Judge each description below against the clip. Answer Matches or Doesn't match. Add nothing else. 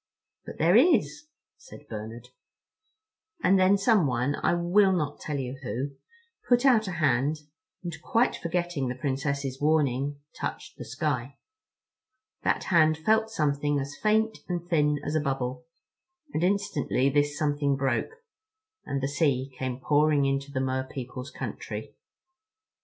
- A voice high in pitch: Doesn't match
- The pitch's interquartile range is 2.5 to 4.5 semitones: Doesn't match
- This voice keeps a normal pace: Doesn't match